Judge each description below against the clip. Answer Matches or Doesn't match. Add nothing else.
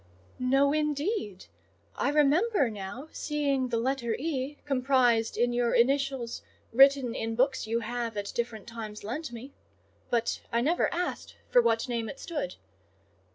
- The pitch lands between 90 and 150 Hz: Doesn't match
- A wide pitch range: Doesn't match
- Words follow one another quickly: Doesn't match